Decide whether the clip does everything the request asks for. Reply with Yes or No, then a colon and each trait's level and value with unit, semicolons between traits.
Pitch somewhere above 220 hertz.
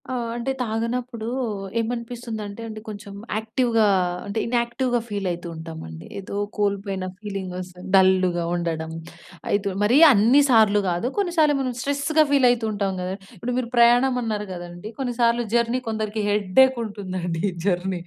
No: high, 215 Hz